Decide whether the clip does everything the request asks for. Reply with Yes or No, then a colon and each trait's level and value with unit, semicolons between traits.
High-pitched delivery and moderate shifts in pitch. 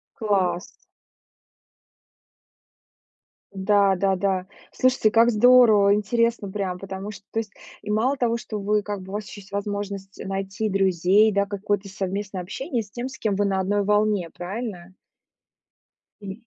No: high, 200 Hz; narrow, 1.8 semitones